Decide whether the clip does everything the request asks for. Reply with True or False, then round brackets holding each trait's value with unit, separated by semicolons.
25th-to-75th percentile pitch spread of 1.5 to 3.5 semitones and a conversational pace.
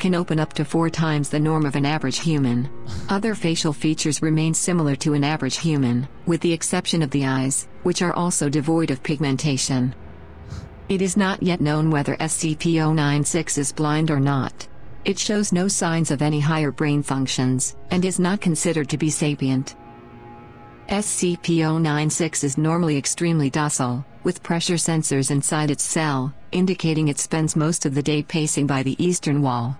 True (3.2 semitones; 170 wpm)